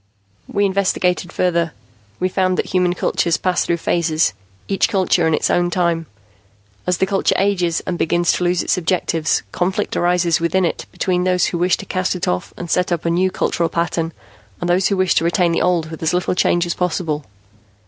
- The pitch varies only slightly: Yes, narrow, 1.5 semitones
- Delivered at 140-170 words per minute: No, average, 200 wpm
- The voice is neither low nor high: Yes, medium, 175 Hz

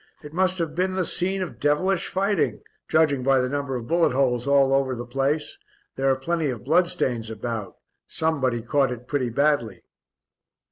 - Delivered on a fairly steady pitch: No, average, 4.8 semitones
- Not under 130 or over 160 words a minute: No, average, 175 wpm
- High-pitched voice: No, medium, 140 Hz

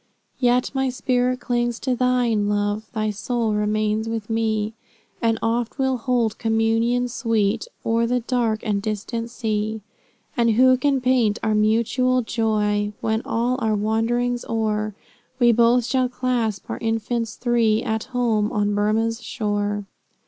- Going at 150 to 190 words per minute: No, average, 140 wpm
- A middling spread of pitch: No, narrow, 2.3 semitones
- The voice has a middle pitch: No, high, 225 Hz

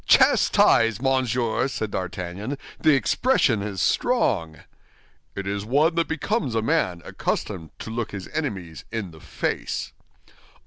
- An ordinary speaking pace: No, slow, 130 wpm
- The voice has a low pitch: Yes, low, 110 Hz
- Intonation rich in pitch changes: Yes, wide, 6.0 semitones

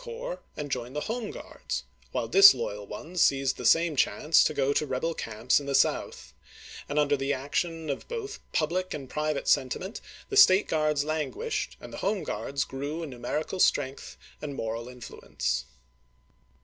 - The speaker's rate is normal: Yes, average, 170 wpm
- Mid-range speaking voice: Yes, medium, 150 Hz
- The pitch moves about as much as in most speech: Yes, average, 4.5 semitones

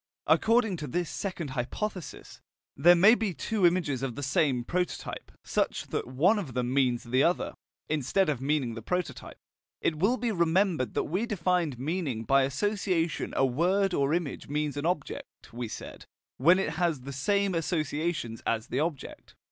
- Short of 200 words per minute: Yes, average, 170 wpm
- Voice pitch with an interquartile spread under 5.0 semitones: No, wide, 5.4 semitones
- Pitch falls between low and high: Yes, medium, 160 Hz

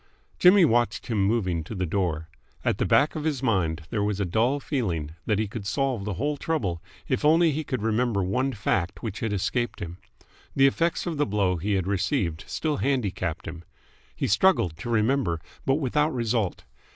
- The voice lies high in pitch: No, low, 110 Hz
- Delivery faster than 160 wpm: Yes, average, 190 wpm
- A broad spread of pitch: Yes, wide, 6.6 semitones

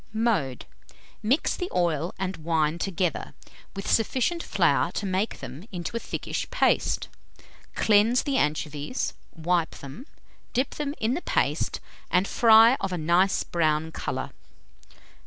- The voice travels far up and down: Yes, wide, 6.3 semitones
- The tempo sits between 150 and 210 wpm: No, slow, 135 wpm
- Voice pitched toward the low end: No, medium, 185 Hz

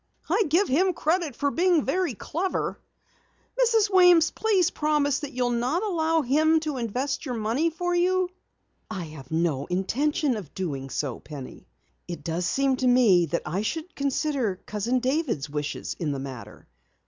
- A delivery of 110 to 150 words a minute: No, average, 160 wpm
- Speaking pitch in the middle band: No, very high, 270 Hz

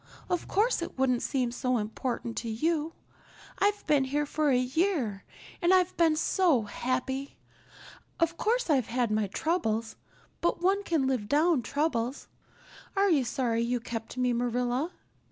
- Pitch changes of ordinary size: No, wide, 5.8 semitones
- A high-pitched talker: Yes, very high, 265 Hz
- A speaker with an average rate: Yes, average, 155 wpm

